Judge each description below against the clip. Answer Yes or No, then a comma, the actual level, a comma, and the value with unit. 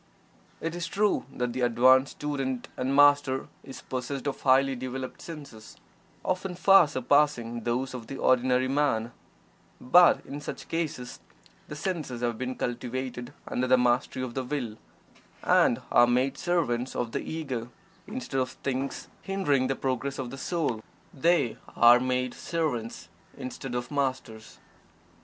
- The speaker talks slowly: No, average, 145 wpm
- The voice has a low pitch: Yes, low, 130 Hz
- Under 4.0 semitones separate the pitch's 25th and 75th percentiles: Yes, average, 2.8 semitones